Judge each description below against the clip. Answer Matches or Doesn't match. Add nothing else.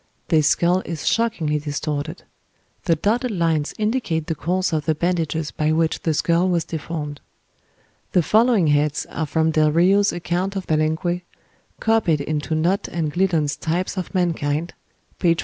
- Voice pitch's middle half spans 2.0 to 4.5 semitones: Matches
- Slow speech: Doesn't match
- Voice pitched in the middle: Matches